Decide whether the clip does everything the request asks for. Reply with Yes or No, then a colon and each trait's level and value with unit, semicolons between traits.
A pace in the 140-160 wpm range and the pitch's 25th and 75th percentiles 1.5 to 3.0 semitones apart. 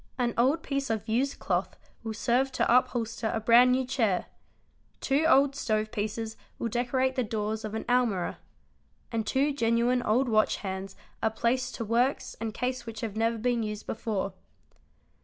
No: average, 175 wpm; narrow, 2.5 semitones